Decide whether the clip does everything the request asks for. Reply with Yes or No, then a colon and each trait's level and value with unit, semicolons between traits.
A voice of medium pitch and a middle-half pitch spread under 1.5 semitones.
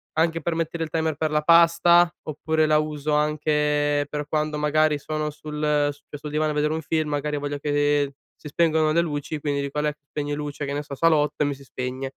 Yes: medium, 150 Hz; narrow, 1.1 semitones